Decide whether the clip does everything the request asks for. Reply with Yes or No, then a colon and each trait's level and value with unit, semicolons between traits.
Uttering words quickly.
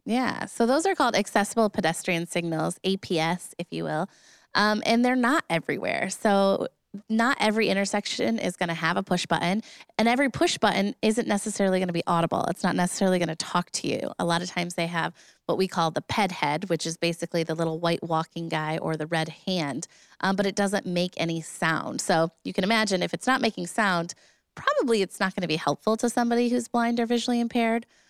Yes: fast, 215 wpm